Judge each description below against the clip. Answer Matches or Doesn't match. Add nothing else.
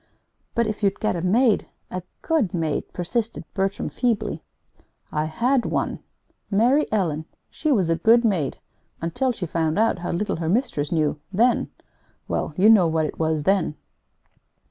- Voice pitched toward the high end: Matches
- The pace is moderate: Matches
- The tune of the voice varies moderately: Doesn't match